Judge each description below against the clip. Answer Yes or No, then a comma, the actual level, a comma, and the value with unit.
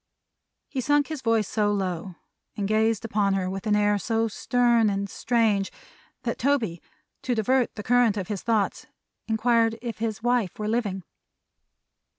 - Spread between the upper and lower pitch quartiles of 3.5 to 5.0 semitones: No, average, 2.8 semitones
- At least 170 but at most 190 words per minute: No, average, 160 wpm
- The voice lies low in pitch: No, high, 220 Hz